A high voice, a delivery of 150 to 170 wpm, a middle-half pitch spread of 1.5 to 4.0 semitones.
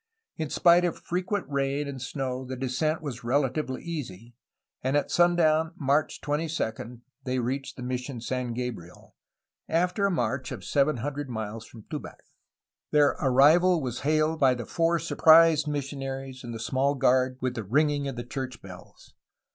No: low, 135 Hz; average, 155 wpm; average, 3.6 semitones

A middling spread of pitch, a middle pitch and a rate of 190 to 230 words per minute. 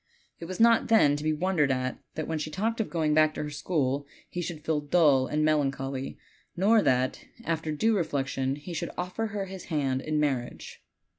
Yes: average, 4.2 semitones; medium, 155 Hz; fast, 205 wpm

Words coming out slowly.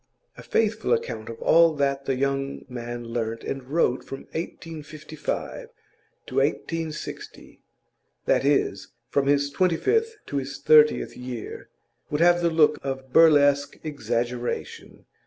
Yes: slow, 130 wpm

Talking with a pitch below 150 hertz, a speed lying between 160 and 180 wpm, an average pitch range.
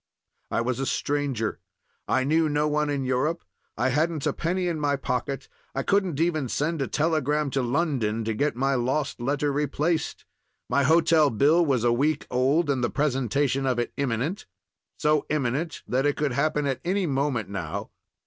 Yes: medium, 140 Hz; average, 175 wpm; average, 3.3 semitones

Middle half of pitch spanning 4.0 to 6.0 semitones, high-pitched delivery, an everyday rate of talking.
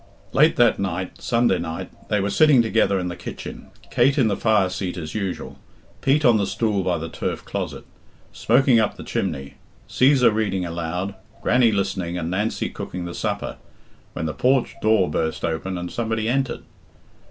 No: average, 4.7 semitones; low, 100 Hz; average, 175 wpm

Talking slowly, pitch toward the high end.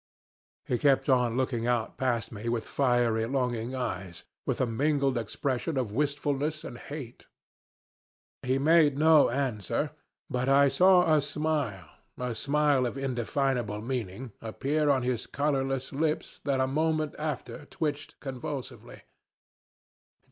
No: slow, 130 wpm; low, 135 Hz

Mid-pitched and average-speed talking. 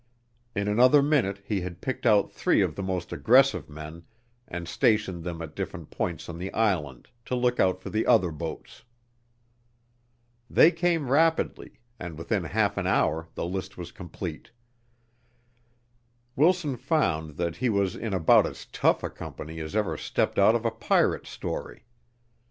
No: very low, 95 Hz; average, 160 wpm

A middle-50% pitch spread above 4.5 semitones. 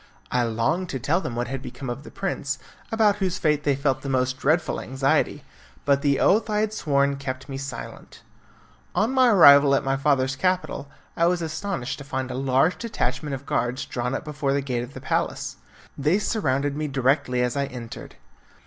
No: average, 3.8 semitones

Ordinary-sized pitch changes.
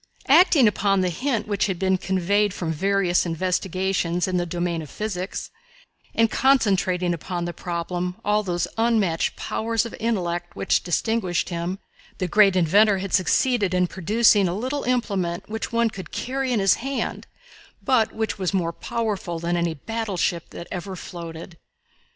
Yes: average, 3.9 semitones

